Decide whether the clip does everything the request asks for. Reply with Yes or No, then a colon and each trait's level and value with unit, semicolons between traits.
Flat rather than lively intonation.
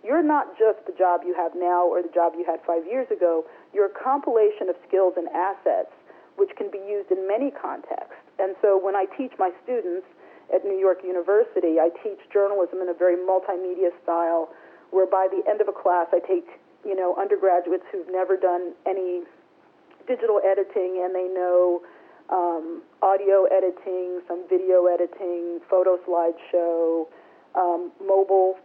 Yes: narrow, 2.2 semitones